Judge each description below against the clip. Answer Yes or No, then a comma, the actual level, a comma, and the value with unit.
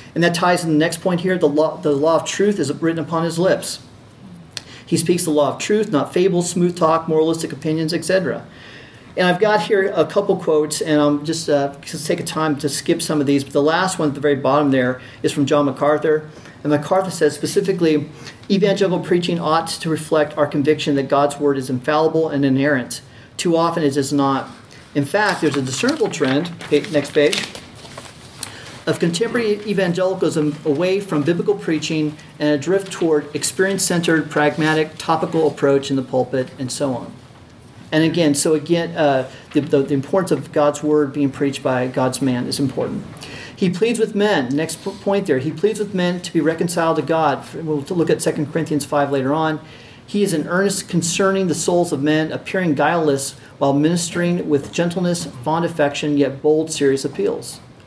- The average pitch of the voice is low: No, medium, 155 Hz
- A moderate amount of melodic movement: Yes, average, 3.2 semitones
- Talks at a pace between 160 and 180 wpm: No, average, 190 wpm